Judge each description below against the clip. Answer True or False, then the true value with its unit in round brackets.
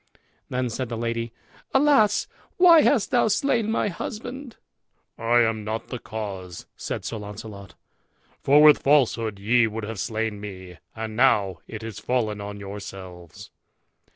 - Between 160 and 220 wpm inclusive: False (145 wpm)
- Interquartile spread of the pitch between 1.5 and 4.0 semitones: False (5.4 semitones)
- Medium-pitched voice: False (115 Hz)